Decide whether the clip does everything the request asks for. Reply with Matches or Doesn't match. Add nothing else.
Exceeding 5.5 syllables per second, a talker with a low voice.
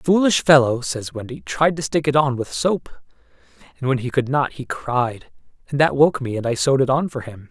Doesn't match